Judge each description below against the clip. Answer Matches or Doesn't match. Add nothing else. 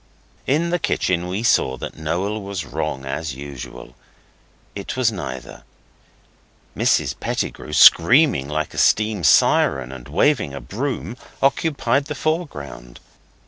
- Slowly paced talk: Matches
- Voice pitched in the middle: Doesn't match